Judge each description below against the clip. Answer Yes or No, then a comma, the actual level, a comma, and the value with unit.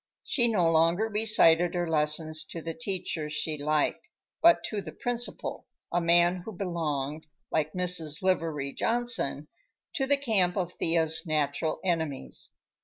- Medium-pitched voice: Yes, medium, 170 Hz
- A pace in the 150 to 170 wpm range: No, average, 140 wpm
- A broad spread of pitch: No, average, 3.9 semitones